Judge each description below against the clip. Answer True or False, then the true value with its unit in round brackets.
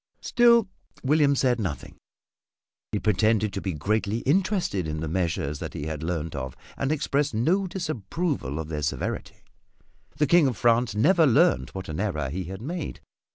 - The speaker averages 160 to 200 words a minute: True (165 wpm)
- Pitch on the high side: False (110 Hz)